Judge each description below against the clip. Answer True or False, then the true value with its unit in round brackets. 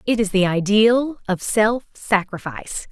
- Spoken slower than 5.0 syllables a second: True (4.2 syllables/s)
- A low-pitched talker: False (210 Hz)